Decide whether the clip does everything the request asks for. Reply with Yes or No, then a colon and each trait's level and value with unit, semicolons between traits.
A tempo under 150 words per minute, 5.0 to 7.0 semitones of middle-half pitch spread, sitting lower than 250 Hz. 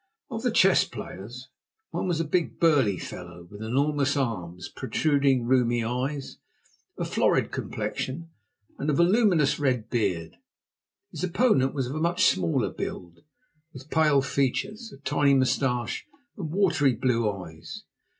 Yes: average, 140 wpm; wide, 5.4 semitones; low, 135 Hz